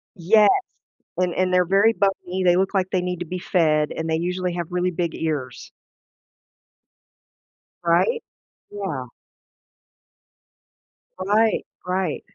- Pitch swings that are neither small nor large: No, narrow, 2.2 semitones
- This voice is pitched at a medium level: Yes, medium, 180 Hz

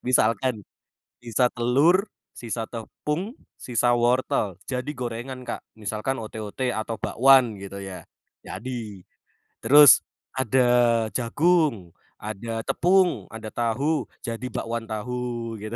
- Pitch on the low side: Yes, low, 120 Hz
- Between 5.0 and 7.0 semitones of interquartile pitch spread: No, average, 2.9 semitones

